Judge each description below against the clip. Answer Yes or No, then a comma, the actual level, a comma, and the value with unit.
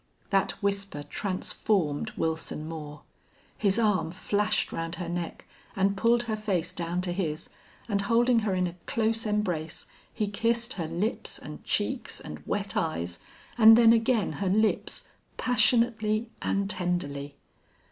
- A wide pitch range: No, average, 4.6 semitones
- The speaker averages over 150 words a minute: No, average, 140 wpm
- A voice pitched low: No, high, 200 Hz